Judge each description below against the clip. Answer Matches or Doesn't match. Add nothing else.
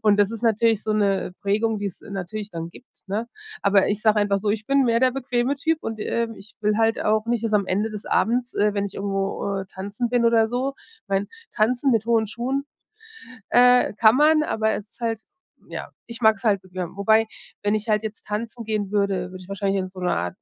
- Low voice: Doesn't match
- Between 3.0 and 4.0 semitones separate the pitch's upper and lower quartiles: Doesn't match